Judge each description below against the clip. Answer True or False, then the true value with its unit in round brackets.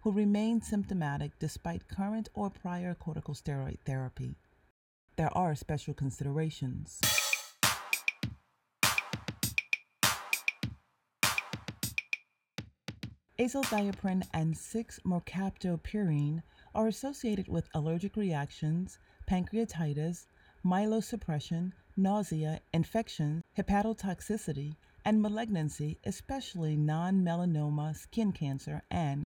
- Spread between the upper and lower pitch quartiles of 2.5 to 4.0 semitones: False (5.0 semitones)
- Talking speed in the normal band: False (70 wpm)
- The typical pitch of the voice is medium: True (170 Hz)